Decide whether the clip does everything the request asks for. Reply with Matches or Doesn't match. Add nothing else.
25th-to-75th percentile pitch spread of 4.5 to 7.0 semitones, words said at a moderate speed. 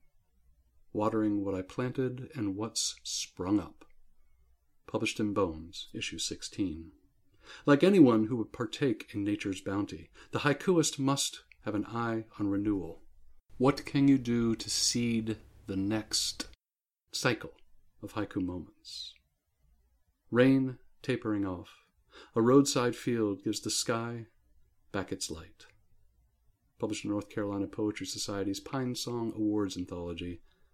Doesn't match